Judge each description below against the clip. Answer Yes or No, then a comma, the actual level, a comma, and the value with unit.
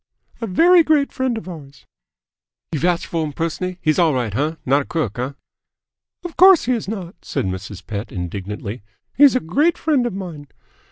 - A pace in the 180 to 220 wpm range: Yes, average, 185 wpm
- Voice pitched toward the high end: No, medium, 165 Hz